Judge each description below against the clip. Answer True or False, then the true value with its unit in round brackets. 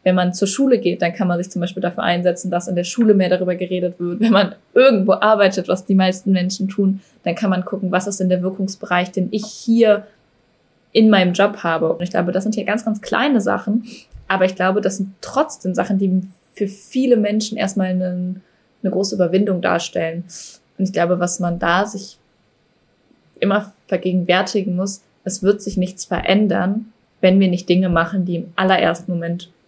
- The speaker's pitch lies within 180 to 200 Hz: True (190 Hz)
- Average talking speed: False (195 wpm)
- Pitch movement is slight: True (2.2 semitones)